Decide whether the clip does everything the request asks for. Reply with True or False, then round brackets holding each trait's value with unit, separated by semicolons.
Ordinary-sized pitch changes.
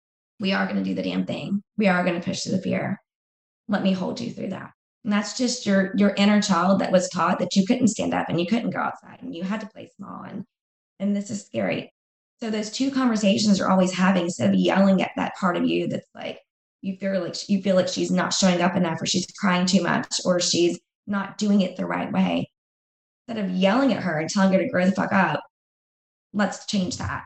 False (2.2 semitones)